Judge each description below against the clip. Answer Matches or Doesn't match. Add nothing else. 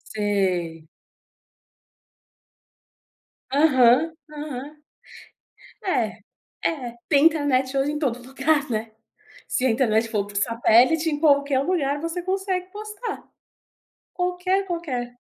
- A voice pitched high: Matches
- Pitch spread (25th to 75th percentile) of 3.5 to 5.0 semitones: Doesn't match